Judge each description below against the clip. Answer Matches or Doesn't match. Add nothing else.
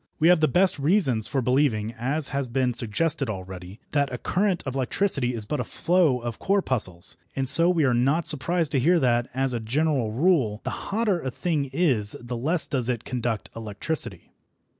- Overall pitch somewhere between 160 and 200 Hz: Doesn't match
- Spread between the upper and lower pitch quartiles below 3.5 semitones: Doesn't match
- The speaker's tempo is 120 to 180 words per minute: Doesn't match